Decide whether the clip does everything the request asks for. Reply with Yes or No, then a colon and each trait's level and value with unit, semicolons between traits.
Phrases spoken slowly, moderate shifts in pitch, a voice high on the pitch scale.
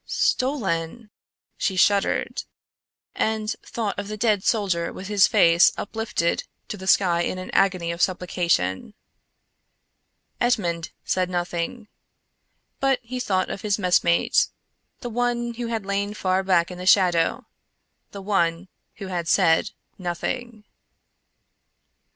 Yes: slow, 125 wpm; average, 3.8 semitones; high, 195 Hz